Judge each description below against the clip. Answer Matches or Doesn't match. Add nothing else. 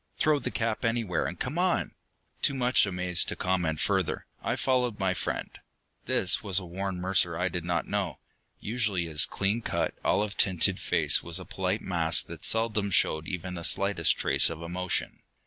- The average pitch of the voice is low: Matches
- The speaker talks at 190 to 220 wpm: Doesn't match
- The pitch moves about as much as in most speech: Matches